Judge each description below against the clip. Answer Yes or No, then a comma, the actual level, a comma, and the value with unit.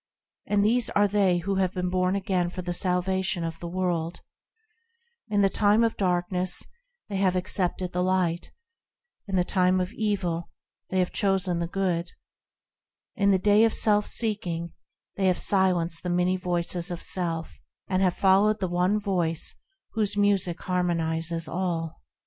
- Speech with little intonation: Yes, narrow, 2.1 semitones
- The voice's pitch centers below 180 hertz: No, medium, 185 Hz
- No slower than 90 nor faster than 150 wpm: No, average, 160 wpm